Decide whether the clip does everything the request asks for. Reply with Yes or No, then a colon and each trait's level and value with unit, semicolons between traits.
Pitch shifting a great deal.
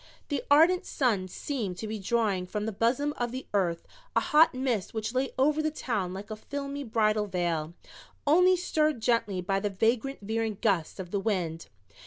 Yes: wide, 5.9 semitones